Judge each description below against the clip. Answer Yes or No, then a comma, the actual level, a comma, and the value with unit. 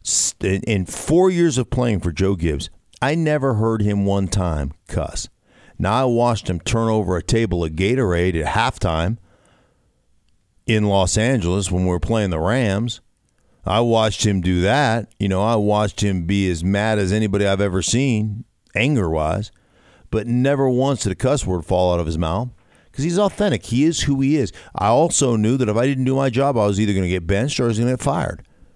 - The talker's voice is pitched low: Yes, low, 105 Hz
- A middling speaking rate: No, fast, 210 wpm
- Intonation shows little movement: No, average, 5.1 semitones